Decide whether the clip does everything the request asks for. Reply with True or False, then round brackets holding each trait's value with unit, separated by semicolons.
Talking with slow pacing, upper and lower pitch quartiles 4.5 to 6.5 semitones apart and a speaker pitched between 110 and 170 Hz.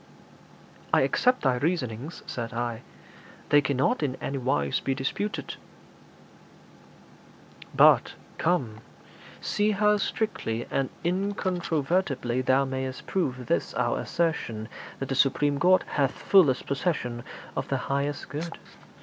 True (115 wpm; 5.6 semitones; 140 Hz)